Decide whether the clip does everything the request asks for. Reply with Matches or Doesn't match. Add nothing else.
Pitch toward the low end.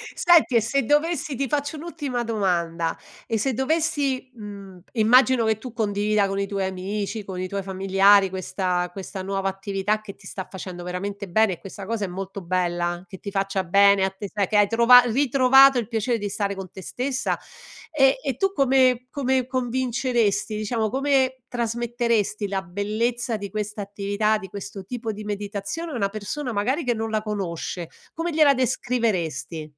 Doesn't match